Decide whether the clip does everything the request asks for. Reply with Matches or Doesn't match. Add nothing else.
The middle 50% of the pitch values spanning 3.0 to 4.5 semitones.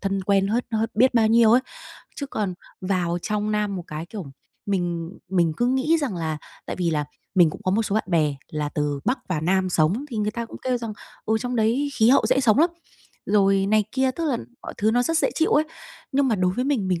Doesn't match